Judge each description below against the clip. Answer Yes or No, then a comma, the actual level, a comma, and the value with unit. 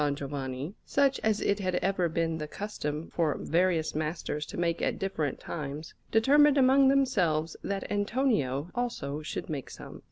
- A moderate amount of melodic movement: No, wide, 6.4 semitones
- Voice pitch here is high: No, medium, 170 Hz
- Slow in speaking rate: No, average, 155 wpm